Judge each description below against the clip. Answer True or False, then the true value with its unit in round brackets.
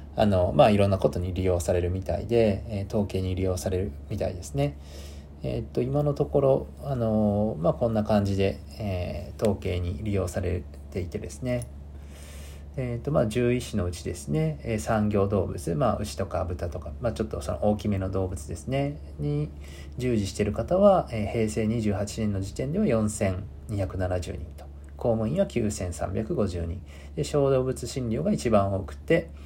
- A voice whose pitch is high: False (95 Hz)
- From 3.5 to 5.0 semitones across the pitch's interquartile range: True (4.6 semitones)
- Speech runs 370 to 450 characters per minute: False (310 characters per minute)